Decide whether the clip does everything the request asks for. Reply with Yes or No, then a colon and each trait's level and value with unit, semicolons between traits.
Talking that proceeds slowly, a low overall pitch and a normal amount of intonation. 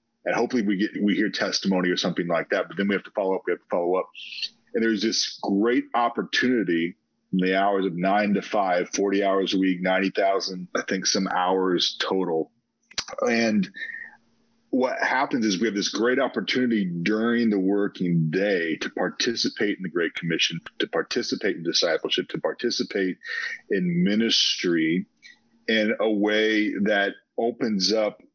No: average, 165 wpm; low, 100 Hz; average, 3.5 semitones